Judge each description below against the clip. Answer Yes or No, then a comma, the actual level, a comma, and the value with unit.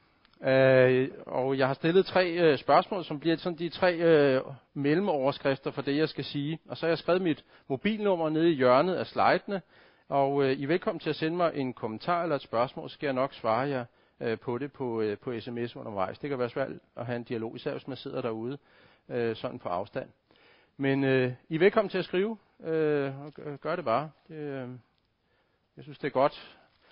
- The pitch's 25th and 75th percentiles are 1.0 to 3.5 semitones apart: No, average, 4.2 semitones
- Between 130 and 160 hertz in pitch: Yes, medium, 140 Hz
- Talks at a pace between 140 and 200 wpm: No, average, 215 wpm